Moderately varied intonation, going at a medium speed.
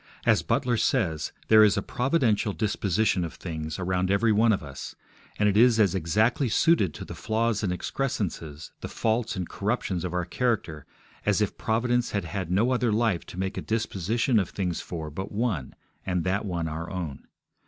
Yes: average, 4.3 semitones; average, 185 wpm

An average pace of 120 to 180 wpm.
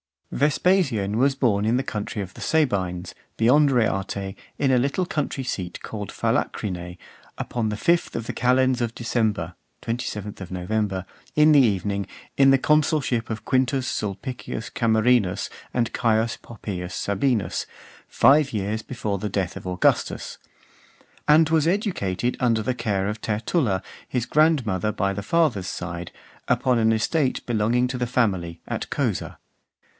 Yes: average, 145 wpm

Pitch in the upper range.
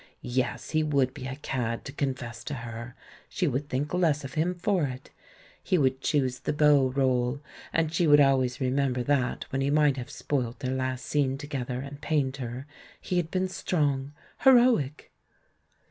No: low, 135 Hz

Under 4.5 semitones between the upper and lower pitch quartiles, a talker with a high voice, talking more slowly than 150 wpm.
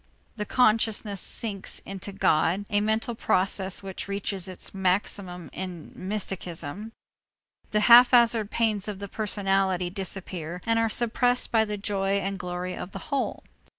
Yes: average, 2.7 semitones; high, 200 Hz; average, 140 wpm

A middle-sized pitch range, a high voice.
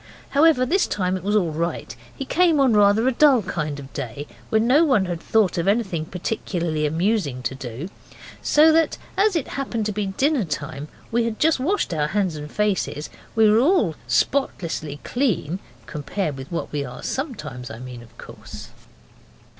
No: wide, 8.9 semitones; high, 195 Hz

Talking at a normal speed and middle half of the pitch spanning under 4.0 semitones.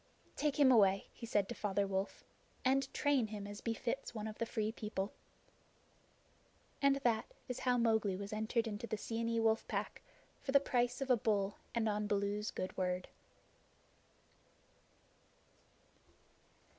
Yes: average, 145 wpm; average, 2.8 semitones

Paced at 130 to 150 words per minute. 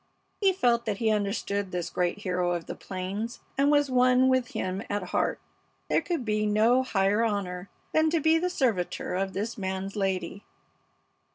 No: average, 175 wpm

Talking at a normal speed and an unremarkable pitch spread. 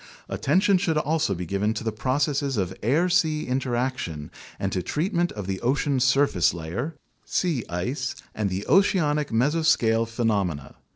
No: average, 155 wpm; wide, 7.1 semitones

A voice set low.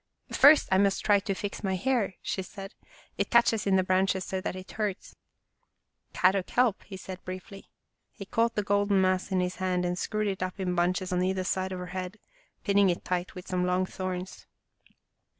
No: high, 190 Hz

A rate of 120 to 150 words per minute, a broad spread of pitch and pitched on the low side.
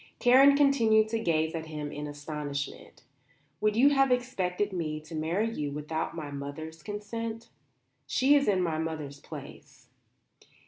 No: average, 145 wpm; wide, 7.1 semitones; medium, 165 Hz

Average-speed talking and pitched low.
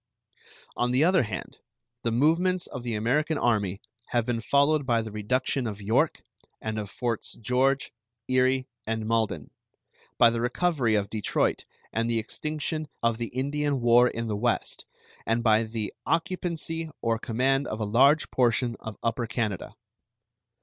Yes: average, 155 wpm; low, 120 Hz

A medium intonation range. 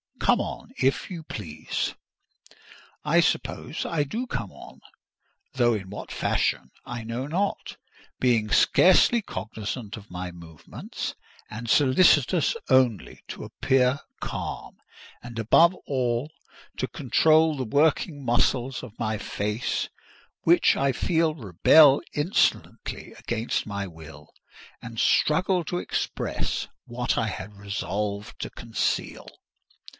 No: wide, 5.9 semitones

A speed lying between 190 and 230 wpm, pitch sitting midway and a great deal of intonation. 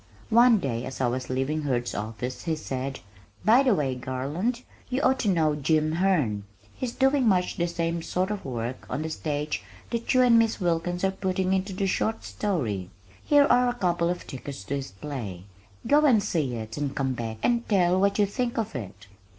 Yes: average, 200 wpm; medium, 165 Hz; wide, 8.0 semitones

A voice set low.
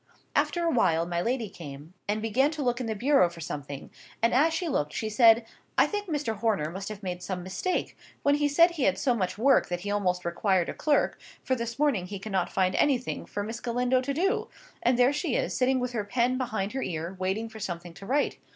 No: high, 225 Hz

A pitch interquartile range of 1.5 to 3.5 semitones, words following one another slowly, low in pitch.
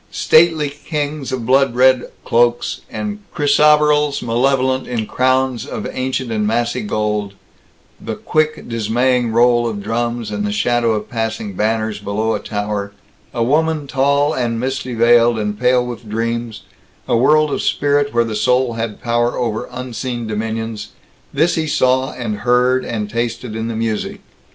No: average, 2.8 semitones; average, 155 wpm; low, 120 Hz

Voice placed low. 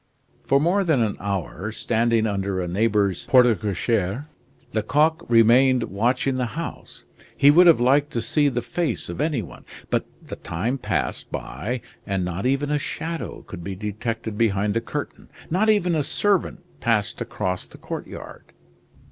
Yes: low, 115 Hz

